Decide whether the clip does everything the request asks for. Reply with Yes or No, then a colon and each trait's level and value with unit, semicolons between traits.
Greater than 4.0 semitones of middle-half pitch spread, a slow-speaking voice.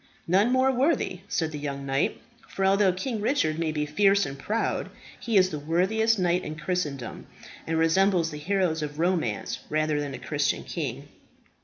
No: average, 4.8 semitones; average, 175 wpm